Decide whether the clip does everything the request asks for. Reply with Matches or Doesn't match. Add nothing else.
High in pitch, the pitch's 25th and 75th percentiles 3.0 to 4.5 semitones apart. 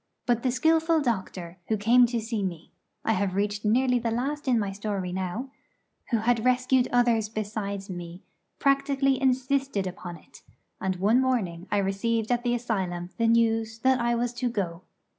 Matches